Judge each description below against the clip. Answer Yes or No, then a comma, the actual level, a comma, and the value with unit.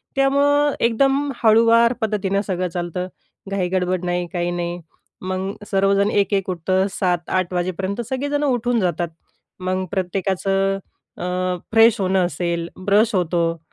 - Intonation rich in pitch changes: No, average, 3.8 semitones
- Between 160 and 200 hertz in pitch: Yes, high, 190 Hz